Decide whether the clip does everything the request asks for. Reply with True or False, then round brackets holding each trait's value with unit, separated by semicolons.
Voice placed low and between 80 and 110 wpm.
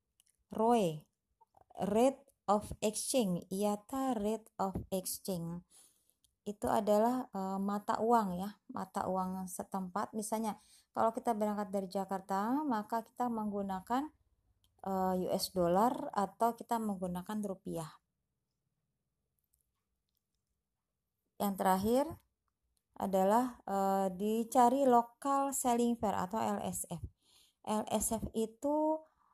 False (215 Hz; 90 wpm)